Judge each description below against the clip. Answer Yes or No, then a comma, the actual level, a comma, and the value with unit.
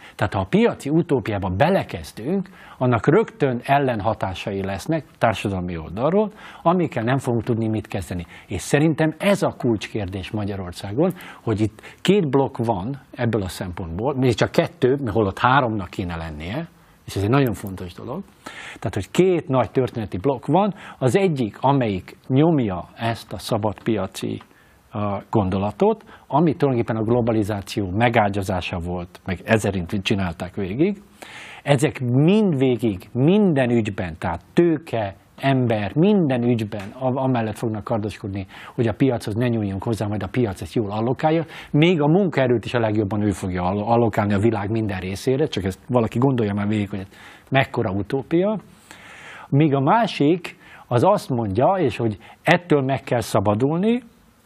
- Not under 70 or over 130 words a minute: No, average, 145 wpm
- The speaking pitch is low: Yes, low, 120 Hz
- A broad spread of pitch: Yes, wide, 5.9 semitones